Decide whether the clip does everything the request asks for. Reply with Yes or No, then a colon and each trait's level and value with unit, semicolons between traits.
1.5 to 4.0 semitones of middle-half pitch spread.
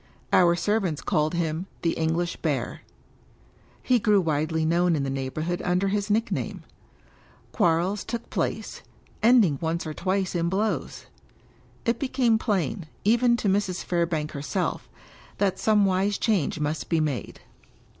No: average, 4.4 semitones